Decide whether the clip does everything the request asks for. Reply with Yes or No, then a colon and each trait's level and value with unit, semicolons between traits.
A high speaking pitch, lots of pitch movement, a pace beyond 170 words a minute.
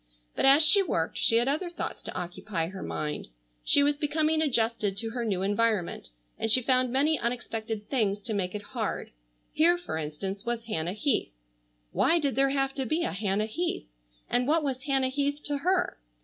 Yes: high, 245 Hz; wide, 5.8 semitones; average, 190 wpm